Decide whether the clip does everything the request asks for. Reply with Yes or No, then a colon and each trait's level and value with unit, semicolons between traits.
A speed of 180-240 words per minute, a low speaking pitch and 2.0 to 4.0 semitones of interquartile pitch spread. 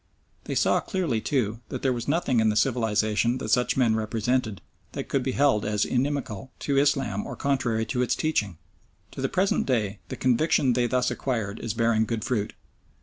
Yes: average, 190 wpm; low, 120 Hz; average, 3.5 semitones